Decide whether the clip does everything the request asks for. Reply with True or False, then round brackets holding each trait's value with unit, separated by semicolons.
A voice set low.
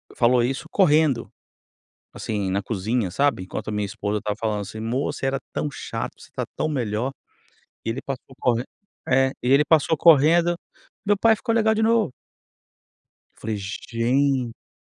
True (125 Hz)